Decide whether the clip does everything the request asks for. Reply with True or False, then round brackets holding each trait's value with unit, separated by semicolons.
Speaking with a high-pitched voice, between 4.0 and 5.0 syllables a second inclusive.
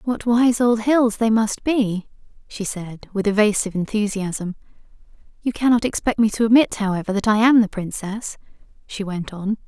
True (215 Hz; 4.9 syllables/s)